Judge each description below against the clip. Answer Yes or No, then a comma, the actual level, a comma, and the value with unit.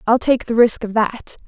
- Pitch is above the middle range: Yes, high, 225 Hz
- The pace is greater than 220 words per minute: Yes, fast, 245 wpm